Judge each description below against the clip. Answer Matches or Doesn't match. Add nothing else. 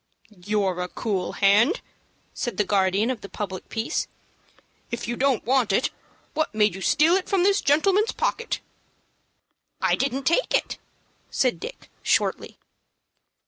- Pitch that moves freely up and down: Matches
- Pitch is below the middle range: Doesn't match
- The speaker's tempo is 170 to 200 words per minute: Doesn't match